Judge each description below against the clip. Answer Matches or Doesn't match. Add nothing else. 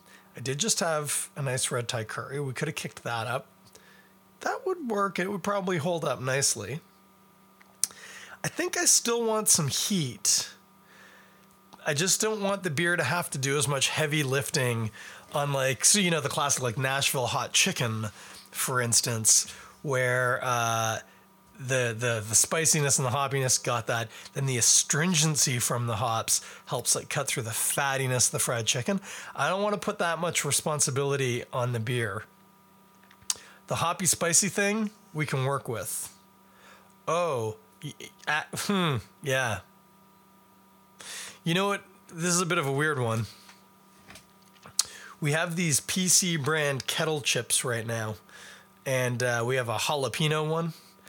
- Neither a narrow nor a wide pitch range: Doesn't match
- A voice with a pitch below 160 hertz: Matches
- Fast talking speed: Doesn't match